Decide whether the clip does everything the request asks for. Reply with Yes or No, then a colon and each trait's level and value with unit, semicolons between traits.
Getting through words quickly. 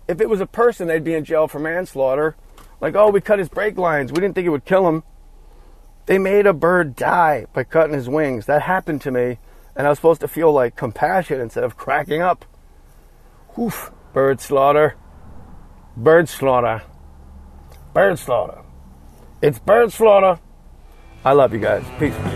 No: average, 175 wpm